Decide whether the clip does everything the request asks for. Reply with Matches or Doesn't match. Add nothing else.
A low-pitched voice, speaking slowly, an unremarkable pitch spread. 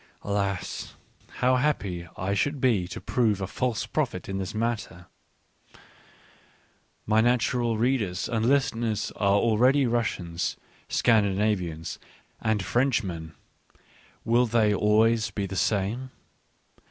Matches